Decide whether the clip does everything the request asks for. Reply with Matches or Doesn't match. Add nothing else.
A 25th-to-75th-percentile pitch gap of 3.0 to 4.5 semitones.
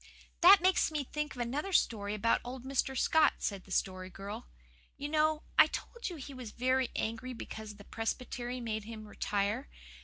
Doesn't match